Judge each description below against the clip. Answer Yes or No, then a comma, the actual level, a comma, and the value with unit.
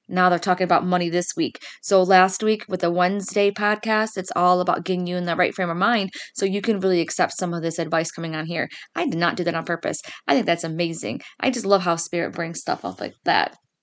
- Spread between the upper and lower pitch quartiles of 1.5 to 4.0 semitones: Yes, narrow, 2.6 semitones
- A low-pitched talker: No, medium, 180 Hz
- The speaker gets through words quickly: Yes, fast, 250 wpm